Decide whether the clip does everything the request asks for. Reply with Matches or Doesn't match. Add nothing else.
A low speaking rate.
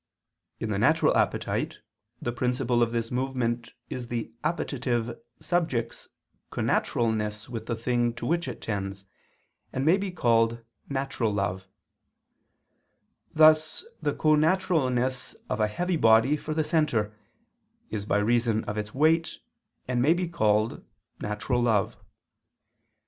Matches